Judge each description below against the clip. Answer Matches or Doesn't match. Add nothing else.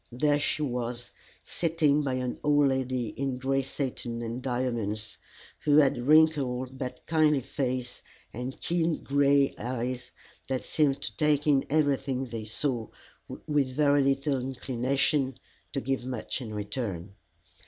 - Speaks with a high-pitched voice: Doesn't match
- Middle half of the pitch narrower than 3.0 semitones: Matches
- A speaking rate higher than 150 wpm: Doesn't match